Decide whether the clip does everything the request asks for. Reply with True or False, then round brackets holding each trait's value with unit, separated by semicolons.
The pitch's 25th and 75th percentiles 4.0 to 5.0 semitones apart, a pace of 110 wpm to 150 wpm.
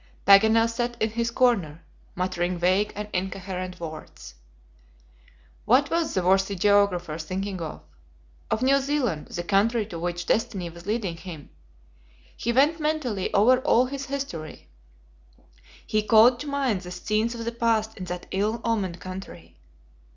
True (4.7 semitones; 145 wpm)